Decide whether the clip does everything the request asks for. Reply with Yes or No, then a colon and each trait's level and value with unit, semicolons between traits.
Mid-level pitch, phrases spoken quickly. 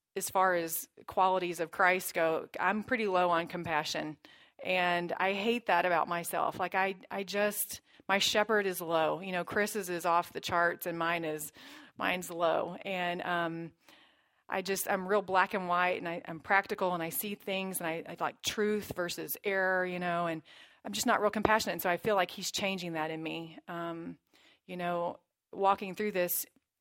No: medium, 180 Hz; average, 190 wpm